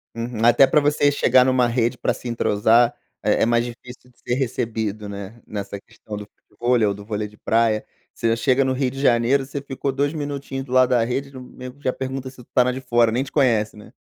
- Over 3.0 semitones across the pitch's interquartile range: No, narrow, 2.6 semitones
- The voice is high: No, low, 125 Hz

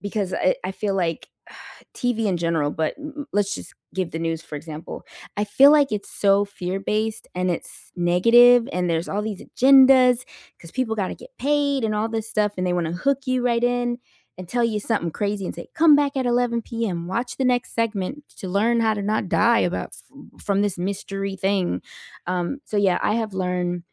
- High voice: Yes, high, 210 Hz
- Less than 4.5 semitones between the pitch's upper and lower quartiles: No, average, 5.0 semitones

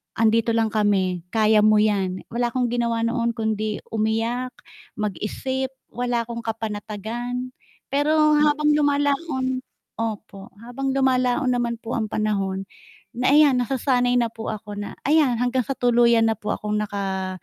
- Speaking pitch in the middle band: No, high, 230 Hz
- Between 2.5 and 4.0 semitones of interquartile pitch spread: Yes, average, 2.9 semitones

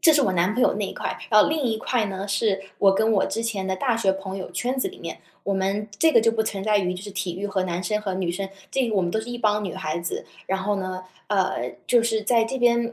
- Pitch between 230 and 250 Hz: No, high, 205 Hz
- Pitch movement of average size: Yes, average, 3.1 semitones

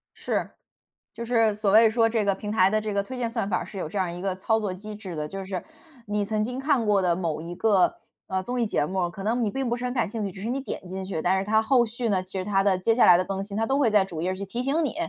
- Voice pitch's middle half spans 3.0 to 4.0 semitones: Yes, average, 3.3 semitones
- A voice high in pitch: Yes, high, 205 Hz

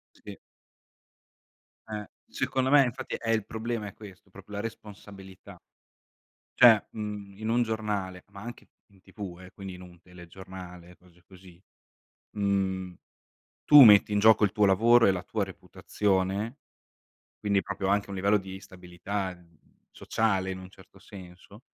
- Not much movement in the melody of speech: Yes, narrow, 2.3 semitones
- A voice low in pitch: Yes, low, 100 Hz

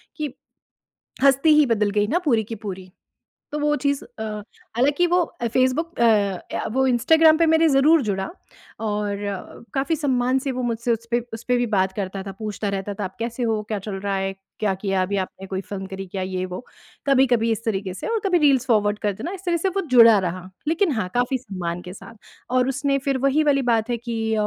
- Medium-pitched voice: No, high, 230 Hz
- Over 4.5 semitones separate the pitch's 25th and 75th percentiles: Yes, wide, 5.6 semitones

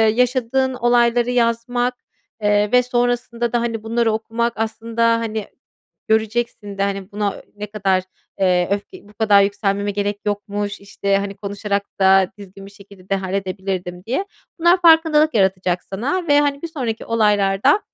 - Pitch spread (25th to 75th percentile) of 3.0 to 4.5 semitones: Yes, average, 3.3 semitones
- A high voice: Yes, high, 210 Hz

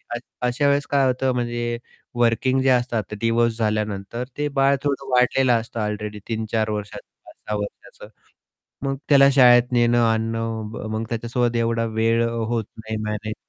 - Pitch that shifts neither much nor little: No, narrow, 2.1 semitones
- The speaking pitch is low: Yes, low, 115 Hz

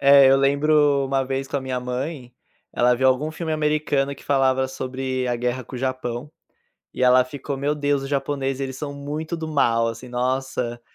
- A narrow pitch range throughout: Yes, narrow, 1.9 semitones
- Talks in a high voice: No, low, 135 Hz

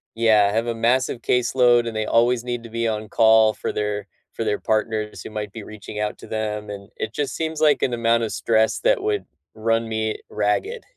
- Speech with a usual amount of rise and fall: No, narrow, 1.9 semitones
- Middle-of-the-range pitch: No, low, 115 Hz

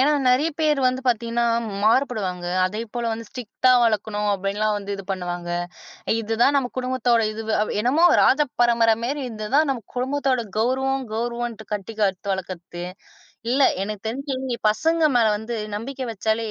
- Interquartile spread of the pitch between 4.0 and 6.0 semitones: No, average, 3.6 semitones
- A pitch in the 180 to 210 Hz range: No, high, 230 Hz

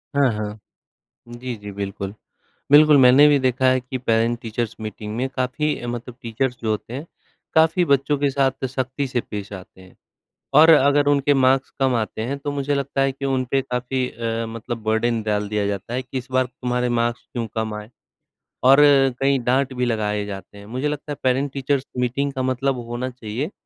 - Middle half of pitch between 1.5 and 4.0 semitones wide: Yes, average, 3.3 semitones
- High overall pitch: No, low, 125 Hz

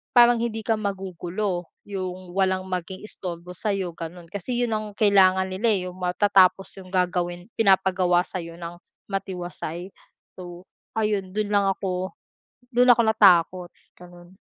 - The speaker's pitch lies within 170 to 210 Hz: Yes, medium, 185 Hz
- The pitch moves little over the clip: Yes, narrow, 2.2 semitones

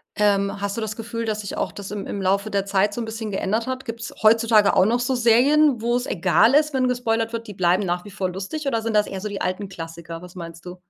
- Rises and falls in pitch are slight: No, average, 3.2 semitones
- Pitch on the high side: Yes, high, 210 Hz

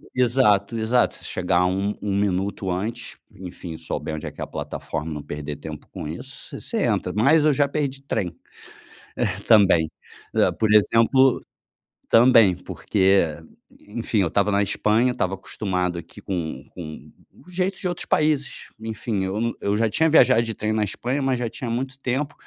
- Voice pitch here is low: Yes, low, 110 Hz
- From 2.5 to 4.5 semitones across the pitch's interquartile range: No, average, 5.2 semitones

